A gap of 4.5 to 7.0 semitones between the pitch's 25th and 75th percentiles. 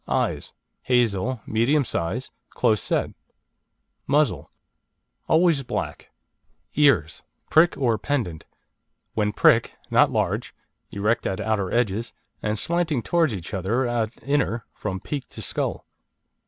Yes: average, 5.1 semitones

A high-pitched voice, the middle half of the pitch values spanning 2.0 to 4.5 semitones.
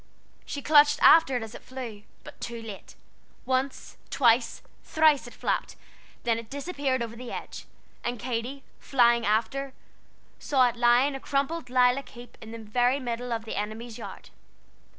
Yes: high, 245 Hz; average, 2.8 semitones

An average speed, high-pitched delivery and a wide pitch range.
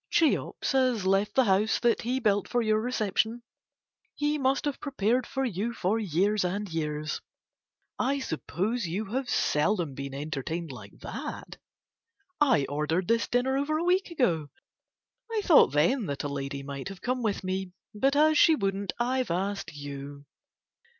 Yes: average, 160 wpm; high, 210 Hz; wide, 7.8 semitones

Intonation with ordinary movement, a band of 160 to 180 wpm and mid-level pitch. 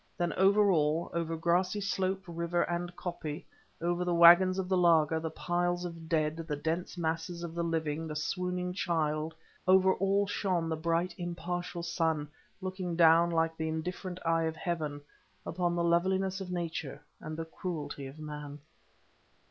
No: narrow, 1.9 semitones; average, 165 wpm; medium, 170 Hz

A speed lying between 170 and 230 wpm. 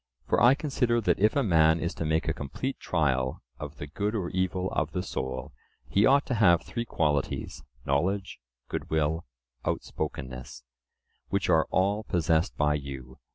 No: average, 160 wpm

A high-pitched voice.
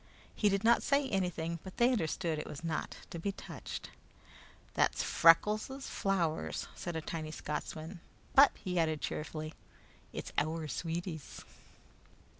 No: medium, 170 Hz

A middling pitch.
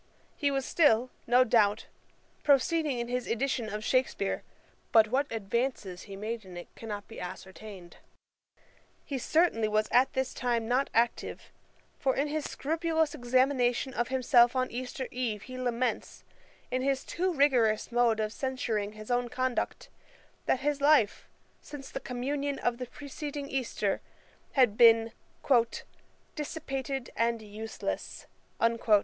No: very high, 250 Hz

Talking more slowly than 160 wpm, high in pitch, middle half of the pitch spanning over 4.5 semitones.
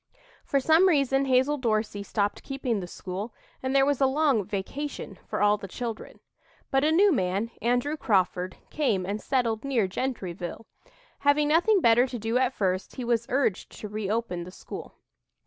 No: average, 170 wpm; high, 235 Hz; average, 5.3 semitones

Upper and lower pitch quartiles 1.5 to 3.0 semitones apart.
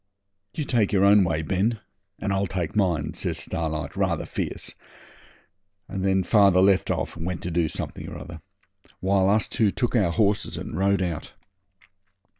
Yes: average, 2.7 semitones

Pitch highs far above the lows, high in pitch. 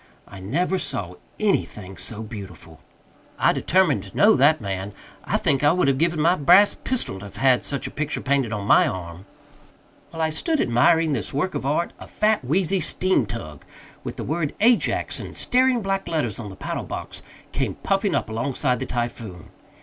No: wide, 8.7 semitones; medium, 140 Hz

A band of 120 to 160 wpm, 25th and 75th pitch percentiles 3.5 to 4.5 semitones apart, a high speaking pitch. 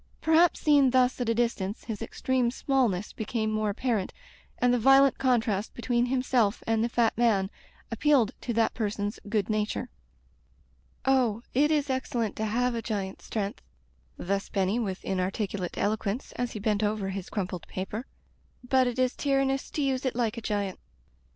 No: average, 175 wpm; average, 3.8 semitones; high, 230 Hz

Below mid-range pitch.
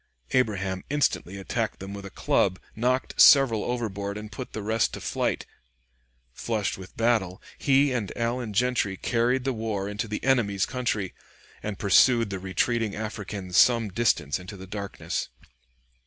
Yes: low, 105 Hz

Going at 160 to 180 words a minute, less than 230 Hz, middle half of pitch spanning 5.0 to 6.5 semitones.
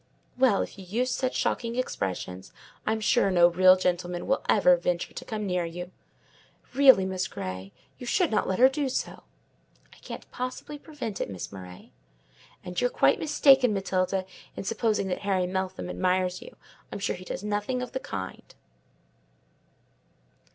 Yes: average, 165 wpm; high, 190 Hz; wide, 5.6 semitones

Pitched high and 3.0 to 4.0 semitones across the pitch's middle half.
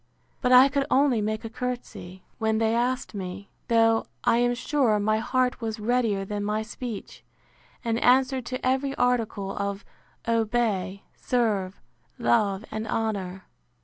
Yes: high, 225 Hz; average, 3.4 semitones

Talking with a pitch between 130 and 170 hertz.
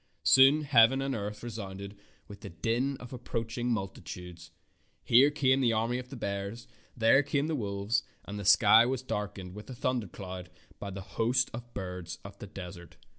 No: low, 115 Hz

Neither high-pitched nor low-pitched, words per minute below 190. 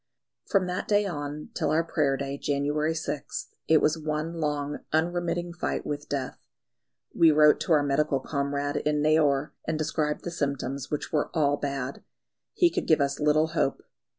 Yes: medium, 150 Hz; average, 170 wpm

